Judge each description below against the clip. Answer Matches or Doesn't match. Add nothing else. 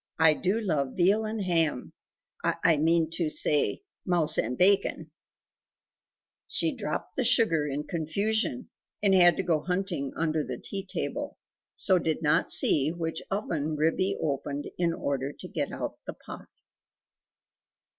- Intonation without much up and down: Doesn't match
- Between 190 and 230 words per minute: Doesn't match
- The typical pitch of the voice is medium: Matches